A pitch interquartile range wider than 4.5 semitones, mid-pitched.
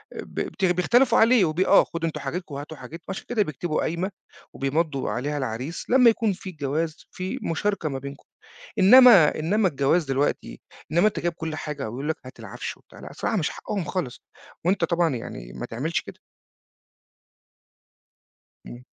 Yes: average, 5.2 semitones; medium, 165 Hz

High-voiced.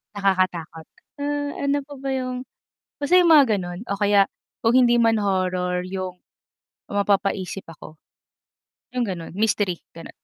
Yes: high, 200 Hz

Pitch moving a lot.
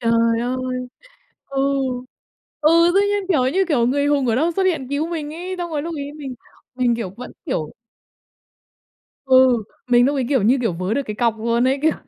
No: average, 4.5 semitones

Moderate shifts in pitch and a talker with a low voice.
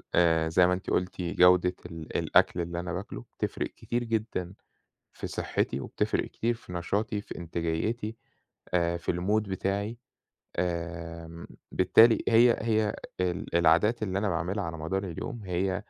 Yes: average, 3.7 semitones; very low, 90 Hz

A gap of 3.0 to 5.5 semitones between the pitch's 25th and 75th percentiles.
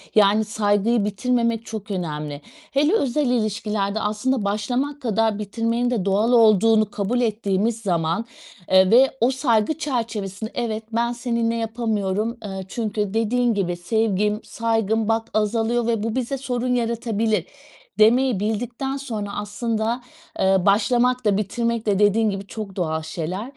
No: narrow, 2.6 semitones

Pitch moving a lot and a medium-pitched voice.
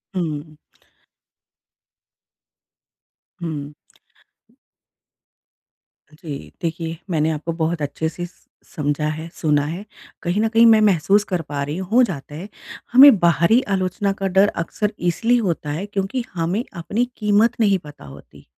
No: average, 4.8 semitones; medium, 175 Hz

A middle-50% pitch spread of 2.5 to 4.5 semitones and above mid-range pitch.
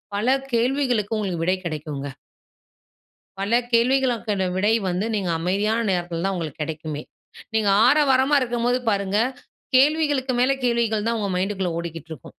No: wide, 5.5 semitones; high, 210 Hz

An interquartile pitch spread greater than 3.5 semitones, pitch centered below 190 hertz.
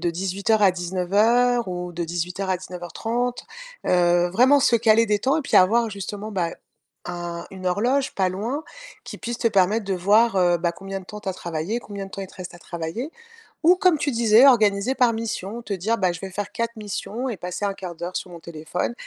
No: average, 4.4 semitones; high, 200 Hz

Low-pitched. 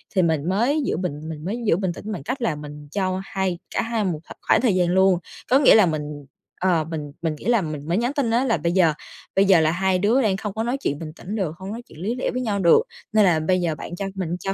No: high, 190 Hz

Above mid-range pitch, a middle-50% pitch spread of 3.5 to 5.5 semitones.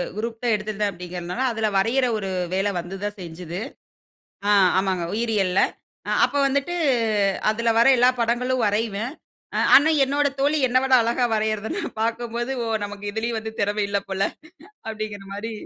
No: high, 220 Hz; average, 3.0 semitones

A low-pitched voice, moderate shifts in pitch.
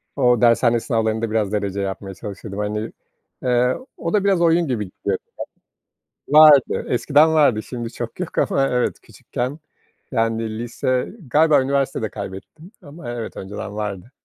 Yes: low, 120 Hz; average, 4.8 semitones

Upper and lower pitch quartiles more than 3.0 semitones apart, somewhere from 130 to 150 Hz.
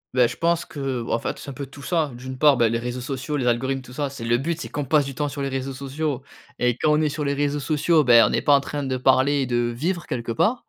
No: average, 2.7 semitones; low, 135 Hz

